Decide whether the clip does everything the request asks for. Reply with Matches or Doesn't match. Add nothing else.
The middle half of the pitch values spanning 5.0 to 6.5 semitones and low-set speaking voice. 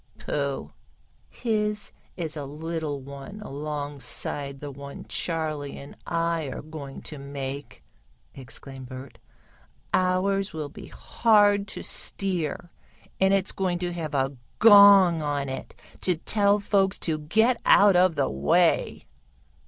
Doesn't match